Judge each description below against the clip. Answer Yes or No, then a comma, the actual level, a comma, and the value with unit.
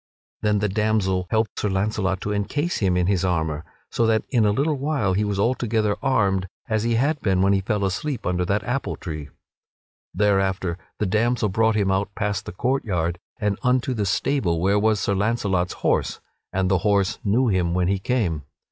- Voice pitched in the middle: No, low, 100 Hz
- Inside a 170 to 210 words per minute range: Yes, average, 195 wpm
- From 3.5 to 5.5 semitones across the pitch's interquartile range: No, average, 3.1 semitones